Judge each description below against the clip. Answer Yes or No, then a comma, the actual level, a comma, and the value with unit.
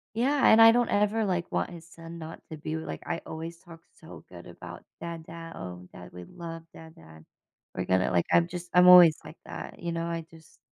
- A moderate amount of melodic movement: No, narrow, 1.9 semitones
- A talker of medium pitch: Yes, medium, 165 Hz